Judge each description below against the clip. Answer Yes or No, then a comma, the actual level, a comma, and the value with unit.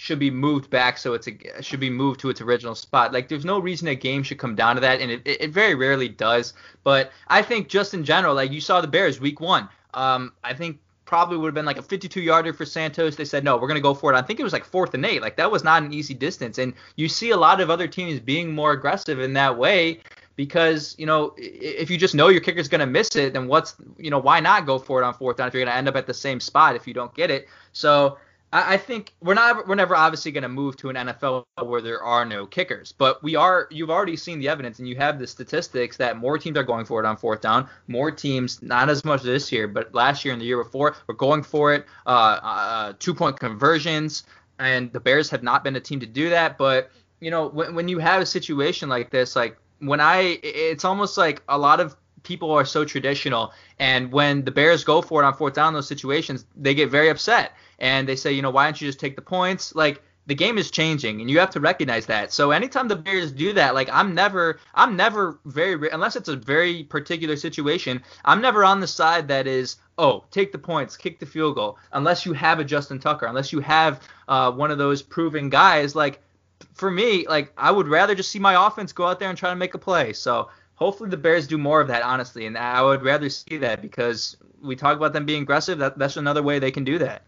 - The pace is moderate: No, fast, 255 wpm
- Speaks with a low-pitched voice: No, medium, 145 Hz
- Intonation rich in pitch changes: No, average, 4.1 semitones